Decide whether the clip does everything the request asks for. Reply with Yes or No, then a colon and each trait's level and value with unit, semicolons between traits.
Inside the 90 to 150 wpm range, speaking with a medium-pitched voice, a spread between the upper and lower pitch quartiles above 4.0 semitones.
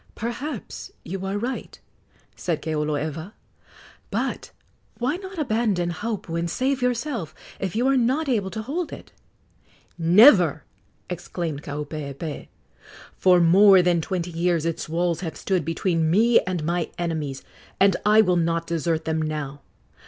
Yes: average, 140 wpm; medium, 175 Hz; average, 5.3 semitones